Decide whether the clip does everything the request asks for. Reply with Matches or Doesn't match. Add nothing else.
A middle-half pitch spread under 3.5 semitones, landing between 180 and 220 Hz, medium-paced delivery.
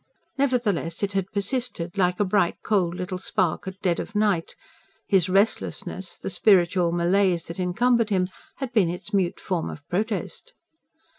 Matches